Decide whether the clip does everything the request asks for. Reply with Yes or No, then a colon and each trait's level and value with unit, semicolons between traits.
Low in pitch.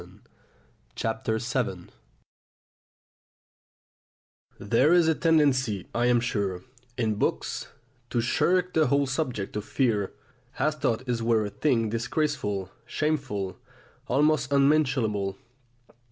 Yes: low, 120 Hz